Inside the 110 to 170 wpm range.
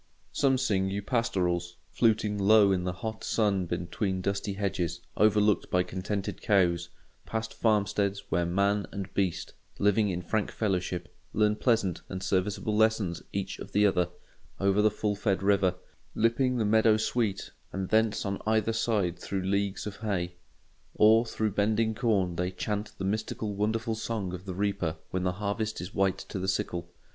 Yes: average, 165 wpm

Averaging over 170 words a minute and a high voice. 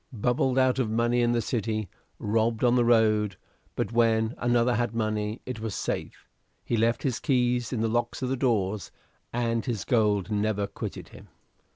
No: average, 180 wpm; low, 115 Hz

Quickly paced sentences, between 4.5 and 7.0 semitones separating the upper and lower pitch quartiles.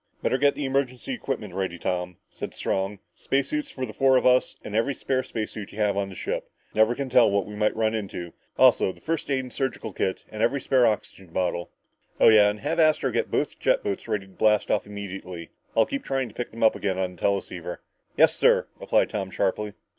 Yes: fast, 225 wpm; average, 5.2 semitones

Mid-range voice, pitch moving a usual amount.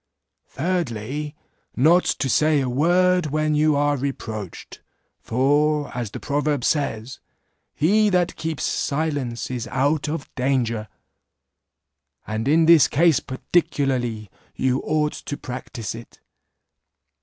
Yes: medium, 145 Hz; average, 3.8 semitones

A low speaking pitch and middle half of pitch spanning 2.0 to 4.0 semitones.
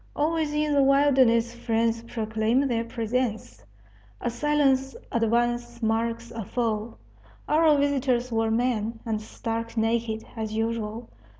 No: high, 235 Hz; narrow, 2.6 semitones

